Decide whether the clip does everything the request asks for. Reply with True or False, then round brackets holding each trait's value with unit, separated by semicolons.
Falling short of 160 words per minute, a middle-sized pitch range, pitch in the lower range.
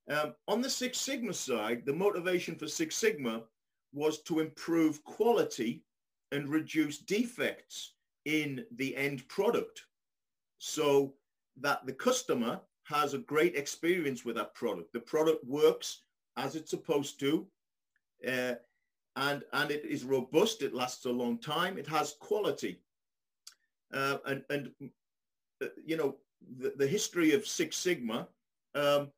False (135 wpm; 4.7 semitones; 150 Hz)